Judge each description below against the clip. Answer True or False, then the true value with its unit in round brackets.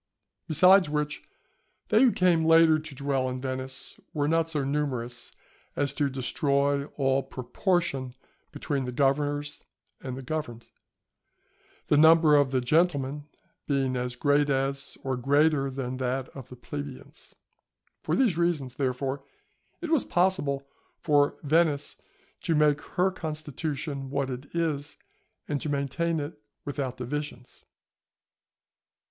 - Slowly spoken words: True (130 wpm)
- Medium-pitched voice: True (145 Hz)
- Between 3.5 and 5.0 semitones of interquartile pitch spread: False (2.7 semitones)